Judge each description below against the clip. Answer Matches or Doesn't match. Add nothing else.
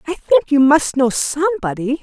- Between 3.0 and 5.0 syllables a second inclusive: Matches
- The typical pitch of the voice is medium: Doesn't match